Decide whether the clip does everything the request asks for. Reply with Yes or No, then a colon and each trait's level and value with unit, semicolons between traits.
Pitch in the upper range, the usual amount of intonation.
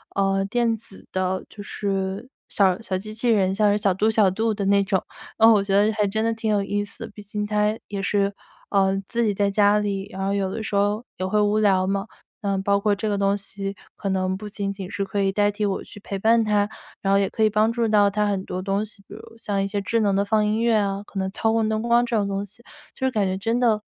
No: high, 205 Hz; narrow, 1.6 semitones